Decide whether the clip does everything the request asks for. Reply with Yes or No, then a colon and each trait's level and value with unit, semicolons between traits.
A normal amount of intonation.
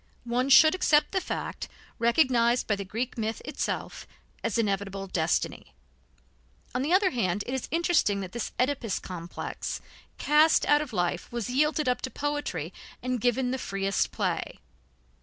No: wide, 6.3 semitones